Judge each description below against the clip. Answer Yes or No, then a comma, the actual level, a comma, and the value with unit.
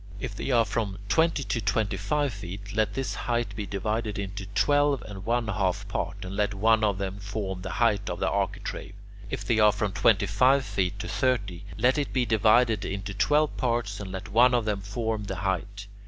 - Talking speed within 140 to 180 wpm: No, fast, 205 wpm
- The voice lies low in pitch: Yes, low, 105 Hz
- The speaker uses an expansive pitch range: No, average, 3.1 semitones